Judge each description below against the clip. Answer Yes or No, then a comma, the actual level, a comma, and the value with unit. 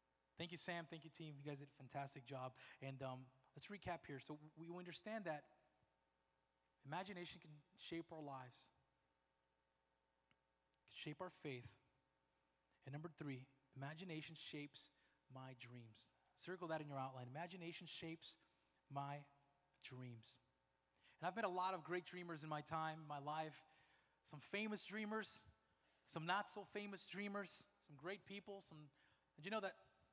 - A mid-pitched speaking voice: Yes, medium, 150 Hz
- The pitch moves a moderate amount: No, wide, 5.8 semitones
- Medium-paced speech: Yes, average, 150 wpm